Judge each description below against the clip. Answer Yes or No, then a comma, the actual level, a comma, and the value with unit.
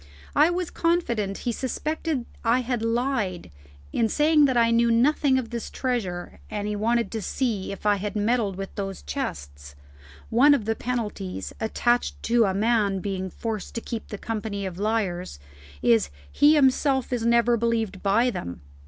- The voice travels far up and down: No, average, 3.8 semitones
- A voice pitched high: Yes, high, 230 Hz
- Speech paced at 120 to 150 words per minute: No, average, 170 wpm